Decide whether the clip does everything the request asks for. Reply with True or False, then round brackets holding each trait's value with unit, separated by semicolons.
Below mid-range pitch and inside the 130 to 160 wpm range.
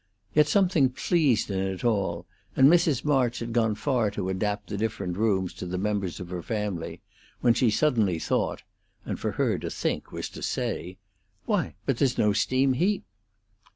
False (110 Hz; 180 wpm)